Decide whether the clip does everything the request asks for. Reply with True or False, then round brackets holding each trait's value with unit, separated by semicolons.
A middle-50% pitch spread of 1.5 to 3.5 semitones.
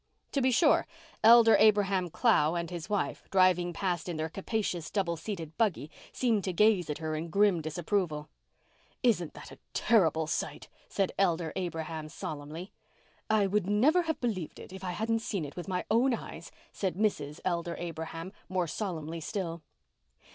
False (4.3 semitones)